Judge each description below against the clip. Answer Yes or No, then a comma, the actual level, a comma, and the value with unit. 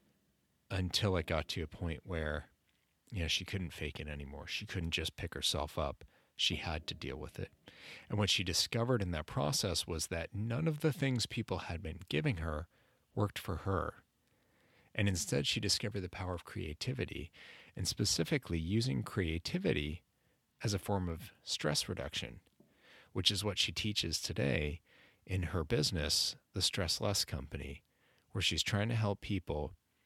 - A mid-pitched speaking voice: No, very low, 95 Hz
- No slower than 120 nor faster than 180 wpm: Yes, average, 170 wpm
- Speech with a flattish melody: No, average, 4.2 semitones